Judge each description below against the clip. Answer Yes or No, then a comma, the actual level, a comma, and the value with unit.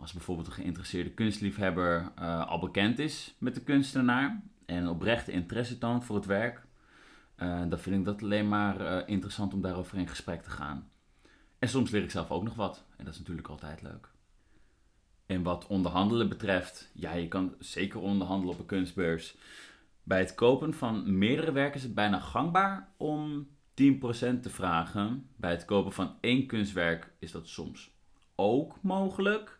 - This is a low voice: Yes, low, 100 Hz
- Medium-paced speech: Yes, average, 170 wpm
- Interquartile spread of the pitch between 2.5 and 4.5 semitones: No, average, 5.3 semitones